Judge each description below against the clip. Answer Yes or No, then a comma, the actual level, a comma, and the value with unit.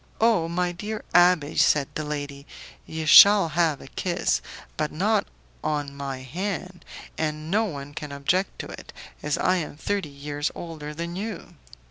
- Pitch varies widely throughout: No, average, 3.8 semitones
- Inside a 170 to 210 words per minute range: No, average, 160 wpm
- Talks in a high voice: No, medium, 160 Hz